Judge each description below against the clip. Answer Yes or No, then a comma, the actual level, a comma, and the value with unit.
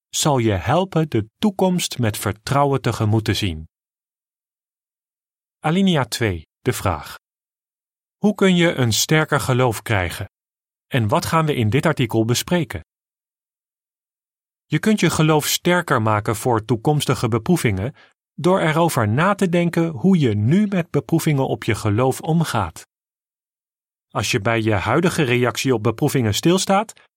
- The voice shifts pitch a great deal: Yes, wide, 6.8 semitones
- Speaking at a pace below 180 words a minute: Yes, slow, 135 wpm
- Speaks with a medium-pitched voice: No, low, 130 Hz